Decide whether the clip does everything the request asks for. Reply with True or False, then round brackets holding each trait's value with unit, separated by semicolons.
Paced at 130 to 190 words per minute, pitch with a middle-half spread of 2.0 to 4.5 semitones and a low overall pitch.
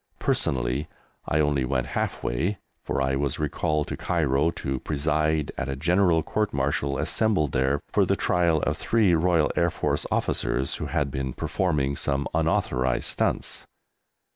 True (155 wpm; 3.4 semitones; 75 Hz)